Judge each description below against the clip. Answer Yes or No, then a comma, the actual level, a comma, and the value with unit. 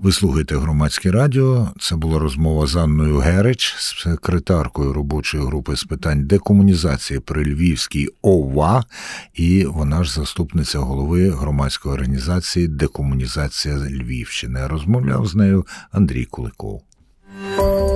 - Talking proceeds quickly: No, slow, 105 wpm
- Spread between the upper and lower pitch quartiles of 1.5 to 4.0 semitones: No, average, 4.6 semitones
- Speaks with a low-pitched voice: Yes, very low, 80 Hz